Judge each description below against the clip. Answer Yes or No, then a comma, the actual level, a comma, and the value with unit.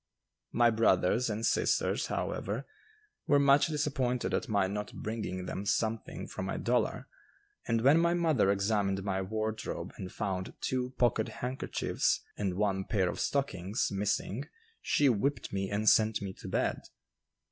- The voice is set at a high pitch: No, low, 110 Hz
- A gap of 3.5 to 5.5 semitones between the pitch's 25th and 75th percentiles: Yes, average, 4.4 semitones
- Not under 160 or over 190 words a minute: No, average, 145 wpm